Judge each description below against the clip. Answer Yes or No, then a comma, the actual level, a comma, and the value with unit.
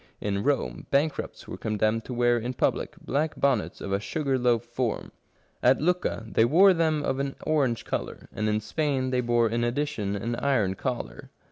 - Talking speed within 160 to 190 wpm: Yes, average, 180 wpm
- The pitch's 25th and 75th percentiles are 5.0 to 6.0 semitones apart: No, average, 3.8 semitones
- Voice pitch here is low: Yes, low, 125 Hz